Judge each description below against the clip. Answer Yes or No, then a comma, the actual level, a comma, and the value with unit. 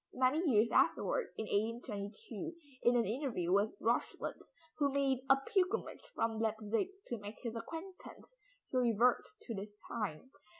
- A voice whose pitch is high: Yes, high, 235 Hz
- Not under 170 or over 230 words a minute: No, average, 140 wpm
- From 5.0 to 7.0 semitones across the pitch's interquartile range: No, average, 4.3 semitones